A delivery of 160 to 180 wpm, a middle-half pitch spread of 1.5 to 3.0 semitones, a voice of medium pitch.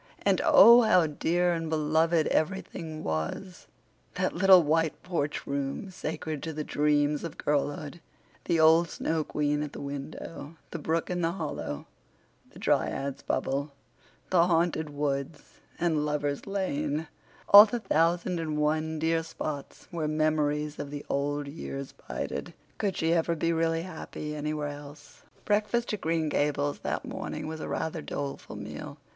No: average, 145 wpm; narrow, 2.4 semitones; medium, 155 Hz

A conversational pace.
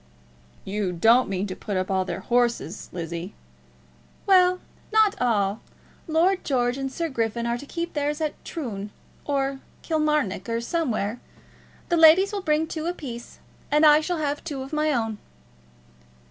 Yes: average, 155 wpm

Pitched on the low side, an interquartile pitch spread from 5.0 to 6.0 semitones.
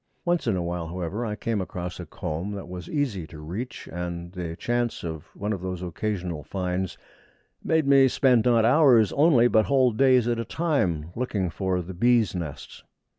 Yes: low, 100 Hz; wide, 5.6 semitones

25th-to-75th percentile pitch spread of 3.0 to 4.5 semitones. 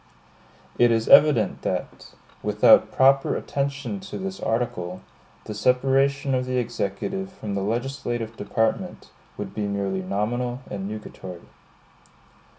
No: average, 4.9 semitones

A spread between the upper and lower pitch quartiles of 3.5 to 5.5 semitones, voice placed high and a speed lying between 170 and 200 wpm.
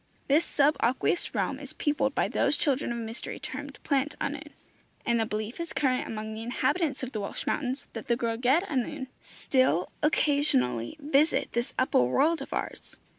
Yes: average, 4.1 semitones; very high, 260 Hz; average, 175 wpm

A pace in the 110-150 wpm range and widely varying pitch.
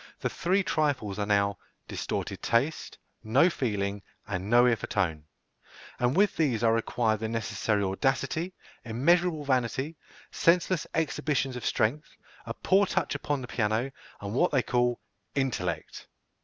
Yes: average, 140 wpm; wide, 5.9 semitones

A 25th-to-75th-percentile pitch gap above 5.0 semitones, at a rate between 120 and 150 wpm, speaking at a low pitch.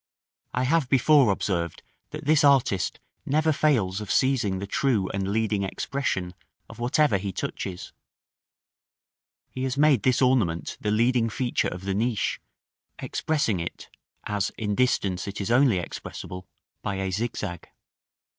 Yes: wide, 5.4 semitones; average, 140 wpm; low, 110 Hz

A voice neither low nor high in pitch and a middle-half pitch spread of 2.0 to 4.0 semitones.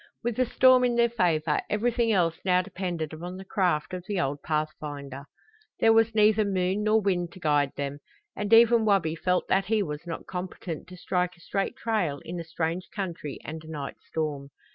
No: medium, 180 Hz; average, 5.0 semitones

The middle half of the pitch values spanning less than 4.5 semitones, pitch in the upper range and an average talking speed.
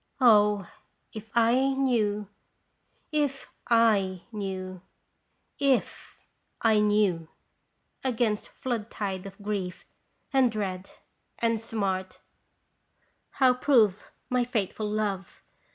No: average, 3.7 semitones; high, 215 Hz; slow, 90 wpm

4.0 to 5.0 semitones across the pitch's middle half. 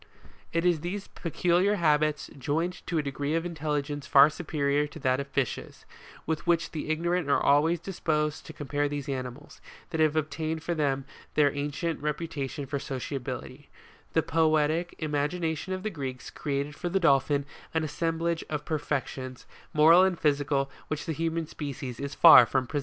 No: narrow, 2.6 semitones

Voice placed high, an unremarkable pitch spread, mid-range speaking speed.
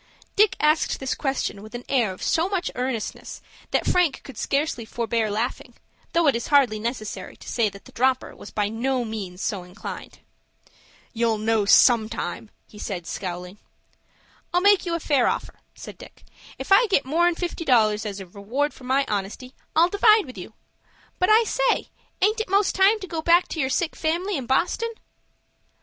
No: very high, 260 Hz; wide, 7.9 semitones; average, 185 wpm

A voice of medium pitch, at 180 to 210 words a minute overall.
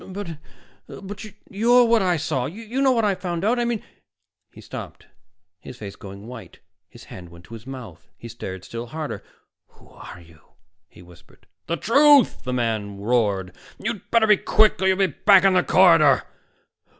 Yes: medium, 160 Hz; average, 185 wpm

